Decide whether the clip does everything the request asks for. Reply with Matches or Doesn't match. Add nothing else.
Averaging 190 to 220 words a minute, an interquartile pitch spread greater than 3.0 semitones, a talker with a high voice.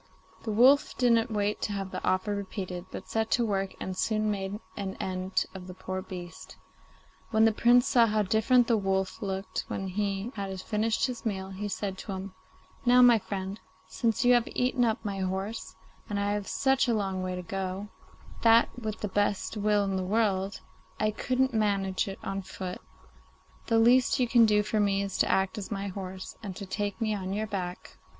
Doesn't match